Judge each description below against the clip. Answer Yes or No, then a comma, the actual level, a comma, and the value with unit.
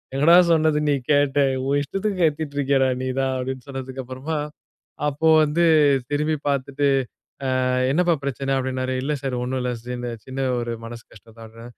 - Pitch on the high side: No, low, 135 Hz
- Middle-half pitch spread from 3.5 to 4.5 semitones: No, narrow, 2.5 semitones